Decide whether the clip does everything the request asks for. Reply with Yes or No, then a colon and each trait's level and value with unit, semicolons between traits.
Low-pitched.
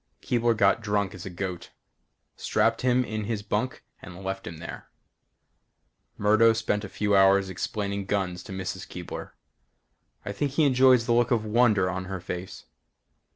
Yes: low, 105 Hz